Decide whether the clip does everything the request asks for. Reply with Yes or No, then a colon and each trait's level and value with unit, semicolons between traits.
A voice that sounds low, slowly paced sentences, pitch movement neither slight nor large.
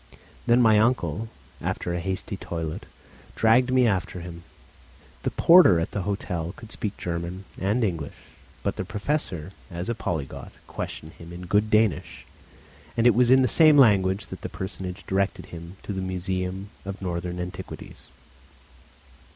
No: very low, 95 Hz; average, 155 wpm; average, 4.0 semitones